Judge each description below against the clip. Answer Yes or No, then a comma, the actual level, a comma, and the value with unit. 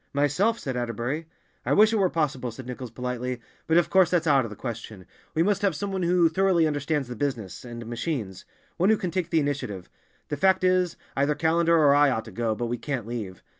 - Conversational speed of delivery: No, fast, 225 wpm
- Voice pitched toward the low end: No, medium, 145 Hz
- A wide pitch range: Yes, wide, 6.2 semitones